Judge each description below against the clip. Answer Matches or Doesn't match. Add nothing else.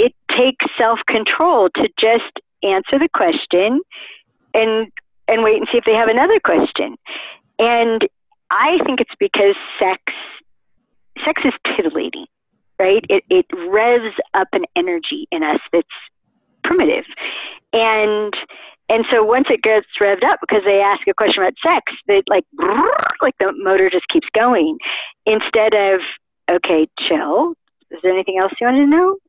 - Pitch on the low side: Doesn't match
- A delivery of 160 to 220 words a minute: Doesn't match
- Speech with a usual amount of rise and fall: Doesn't match